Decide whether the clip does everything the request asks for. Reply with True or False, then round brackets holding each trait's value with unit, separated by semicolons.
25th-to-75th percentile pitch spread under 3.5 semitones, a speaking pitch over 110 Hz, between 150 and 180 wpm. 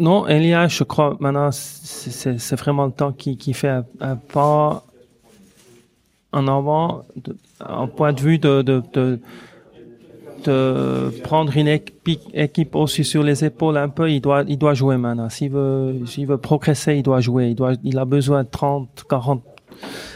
True (2.4 semitones; 140 Hz; 170 wpm)